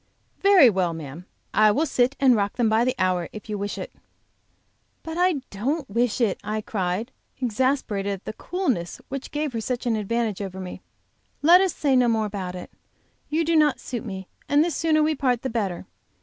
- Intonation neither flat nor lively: No, wide, 5.9 semitones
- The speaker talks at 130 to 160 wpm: No, average, 200 wpm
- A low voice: No, high, 235 Hz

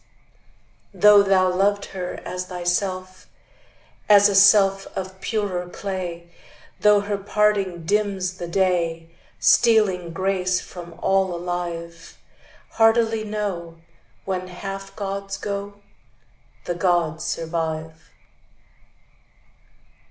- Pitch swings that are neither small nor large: No, narrow, 2.3 semitones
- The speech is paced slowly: Yes, slow, 95 wpm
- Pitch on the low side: No, high, 190 Hz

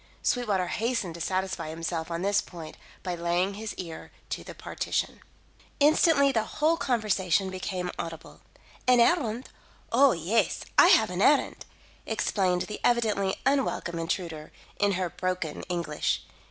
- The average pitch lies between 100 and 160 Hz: No, high, 190 Hz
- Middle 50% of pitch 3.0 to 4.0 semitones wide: No, average, 5.1 semitones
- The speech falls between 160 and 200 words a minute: No, average, 140 wpm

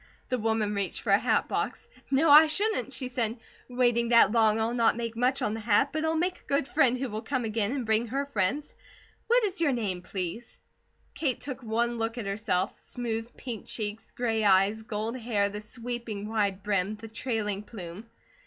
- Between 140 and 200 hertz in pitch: No, high, 230 Hz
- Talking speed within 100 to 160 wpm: No, average, 200 wpm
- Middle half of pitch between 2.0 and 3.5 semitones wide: Yes, average, 3.2 semitones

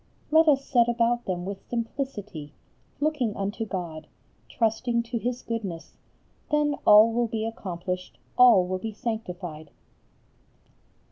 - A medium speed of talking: No, slow, 125 wpm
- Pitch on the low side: No, high, 225 Hz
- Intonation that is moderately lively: Yes, average, 4.5 semitones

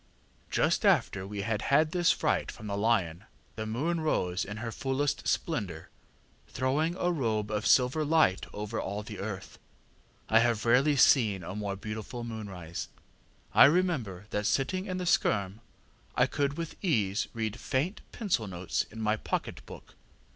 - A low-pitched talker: Yes, low, 110 Hz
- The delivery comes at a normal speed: Yes, average, 160 wpm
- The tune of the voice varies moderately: No, wide, 5.9 semitones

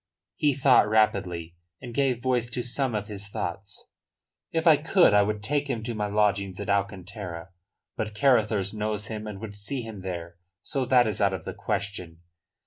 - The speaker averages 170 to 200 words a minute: Yes, average, 185 wpm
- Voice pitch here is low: Yes, low, 105 Hz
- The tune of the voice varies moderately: Yes, average, 3.6 semitones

